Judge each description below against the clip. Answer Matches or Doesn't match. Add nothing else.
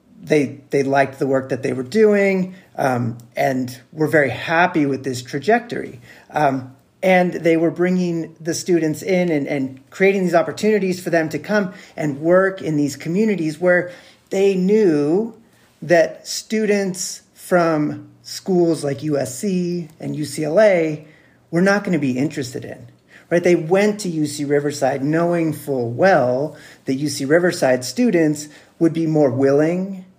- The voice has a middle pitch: Matches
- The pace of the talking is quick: Doesn't match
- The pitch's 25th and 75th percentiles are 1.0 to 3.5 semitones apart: Doesn't match